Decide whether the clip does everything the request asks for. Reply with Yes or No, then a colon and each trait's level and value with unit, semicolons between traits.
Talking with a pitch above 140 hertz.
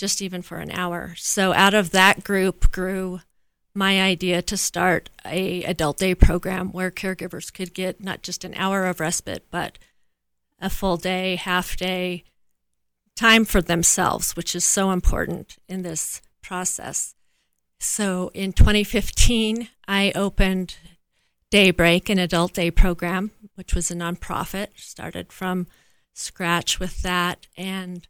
Yes: medium, 185 Hz